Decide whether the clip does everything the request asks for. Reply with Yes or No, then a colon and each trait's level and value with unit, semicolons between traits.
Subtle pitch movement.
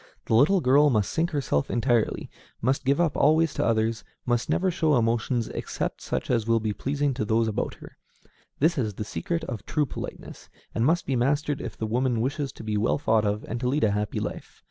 No: average, 4.6 semitones